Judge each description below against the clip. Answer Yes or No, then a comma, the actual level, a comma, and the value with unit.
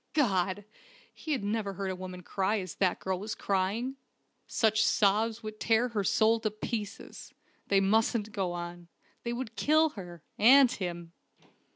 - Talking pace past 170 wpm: No, average, 160 wpm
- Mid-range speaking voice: No, high, 205 Hz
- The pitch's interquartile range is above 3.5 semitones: No, average, 3.2 semitones